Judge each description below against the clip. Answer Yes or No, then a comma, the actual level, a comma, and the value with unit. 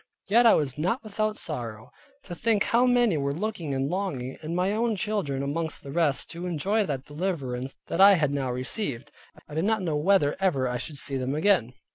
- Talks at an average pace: No, fast, 210 wpm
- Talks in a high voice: No, medium, 160 Hz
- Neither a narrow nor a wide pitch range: No, wide, 6.5 semitones